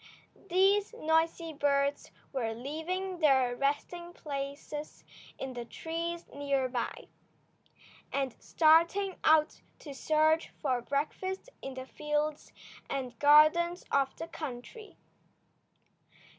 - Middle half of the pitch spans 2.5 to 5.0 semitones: Yes, average, 3.6 semitones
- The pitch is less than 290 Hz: No, very high, 300 Hz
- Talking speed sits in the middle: No, slow, 105 wpm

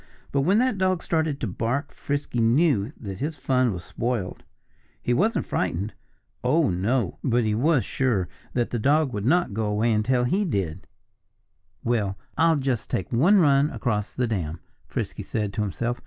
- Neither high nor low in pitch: No, low, 120 Hz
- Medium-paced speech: Yes, average, 170 wpm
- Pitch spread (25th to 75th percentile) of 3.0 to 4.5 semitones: No, wide, 5.6 semitones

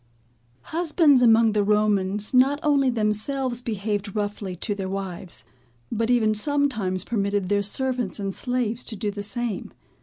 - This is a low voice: No, high, 215 Hz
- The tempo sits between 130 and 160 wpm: Yes, average, 145 wpm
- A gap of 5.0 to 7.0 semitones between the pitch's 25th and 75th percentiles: No, average, 3.6 semitones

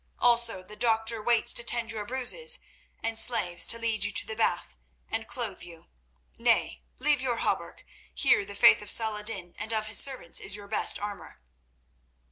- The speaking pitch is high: Yes, high, 225 Hz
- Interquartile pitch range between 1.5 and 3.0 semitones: Yes, narrow, 2.4 semitones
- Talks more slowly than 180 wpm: No, average, 185 wpm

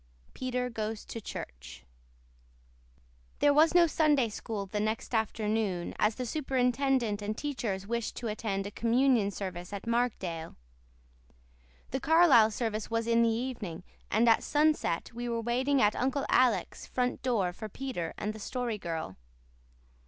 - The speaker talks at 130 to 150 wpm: Yes, average, 145 wpm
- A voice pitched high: Yes, high, 230 Hz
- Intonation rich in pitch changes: No, average, 3.7 semitones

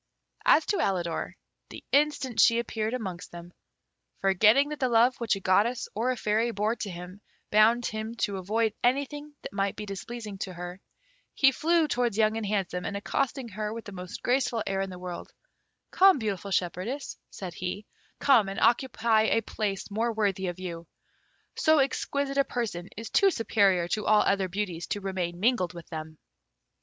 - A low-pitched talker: No, high, 215 Hz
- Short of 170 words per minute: No, average, 180 wpm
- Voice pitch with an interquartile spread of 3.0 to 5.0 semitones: Yes, average, 4.2 semitones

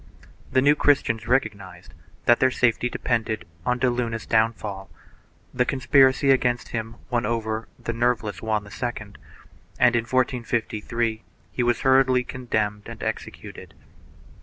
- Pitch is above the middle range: No, low, 120 Hz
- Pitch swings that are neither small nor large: No, narrow, 2.3 semitones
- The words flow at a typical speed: No, slow, 130 wpm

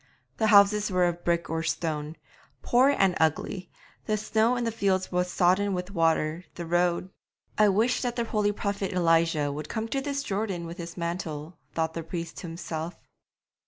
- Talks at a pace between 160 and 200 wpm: Yes, average, 180 wpm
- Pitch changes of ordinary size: Yes, average, 3.9 semitones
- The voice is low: No, medium, 180 Hz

